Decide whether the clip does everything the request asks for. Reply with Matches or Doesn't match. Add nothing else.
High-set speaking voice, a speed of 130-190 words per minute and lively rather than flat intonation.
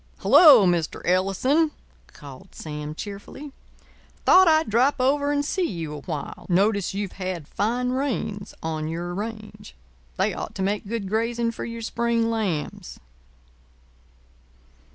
Matches